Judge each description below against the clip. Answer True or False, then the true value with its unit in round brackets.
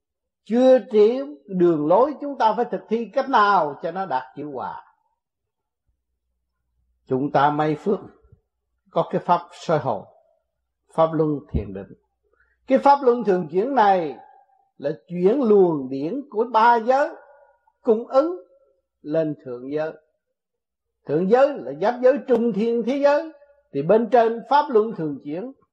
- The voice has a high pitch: True (225 Hz)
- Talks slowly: True (145 wpm)